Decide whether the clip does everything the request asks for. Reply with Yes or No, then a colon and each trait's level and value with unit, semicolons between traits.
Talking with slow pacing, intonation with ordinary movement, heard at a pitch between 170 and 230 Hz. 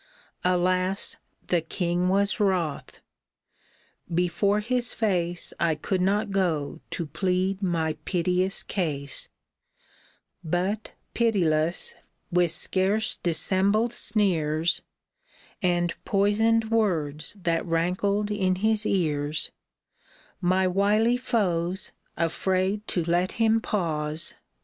Yes: slow, 95 wpm; average, 3.4 semitones; medium, 185 Hz